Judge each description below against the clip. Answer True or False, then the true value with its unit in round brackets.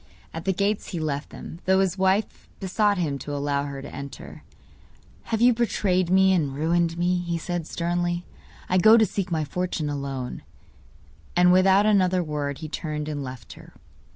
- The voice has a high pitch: False (175 Hz)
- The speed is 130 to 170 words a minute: False (180 wpm)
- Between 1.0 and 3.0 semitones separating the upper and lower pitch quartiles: False (4.2 semitones)